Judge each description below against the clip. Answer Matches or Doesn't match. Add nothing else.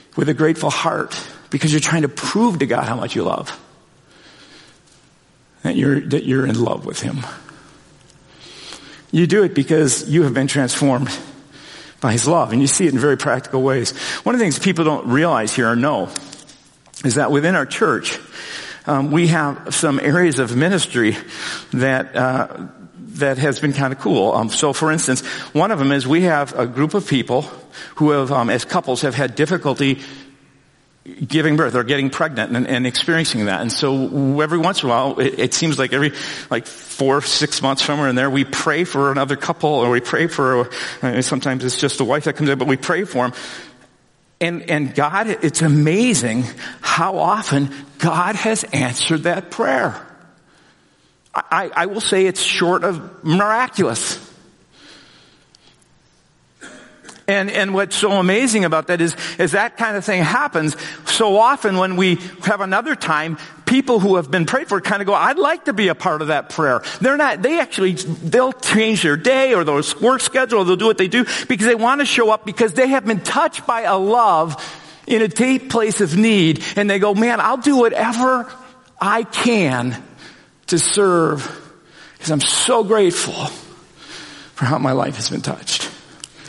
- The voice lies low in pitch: Doesn't match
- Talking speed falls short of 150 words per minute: Doesn't match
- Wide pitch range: Matches